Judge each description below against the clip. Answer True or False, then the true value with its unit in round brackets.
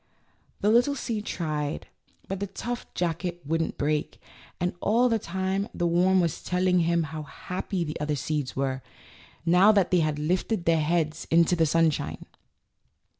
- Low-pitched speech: False (170 Hz)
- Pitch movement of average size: True (3.4 semitones)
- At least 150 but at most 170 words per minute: True (160 wpm)